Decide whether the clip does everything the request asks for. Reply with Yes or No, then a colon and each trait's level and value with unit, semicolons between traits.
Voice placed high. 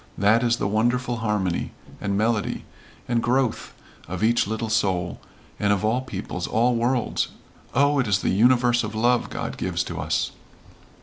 No: low, 115 Hz